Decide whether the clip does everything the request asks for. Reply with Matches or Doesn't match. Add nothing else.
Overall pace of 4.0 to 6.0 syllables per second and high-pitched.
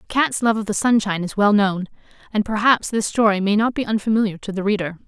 Doesn't match